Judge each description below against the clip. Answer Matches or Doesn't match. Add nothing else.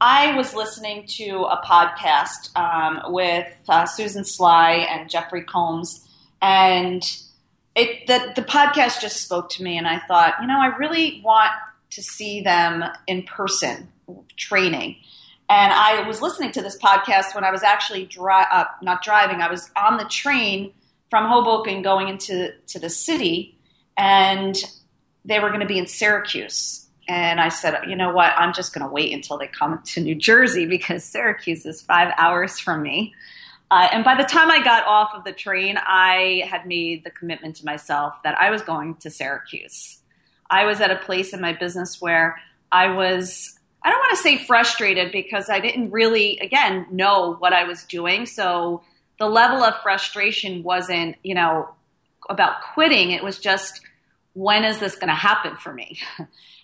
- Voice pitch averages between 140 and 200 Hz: Matches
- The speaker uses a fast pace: Doesn't match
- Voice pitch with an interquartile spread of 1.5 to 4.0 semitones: Matches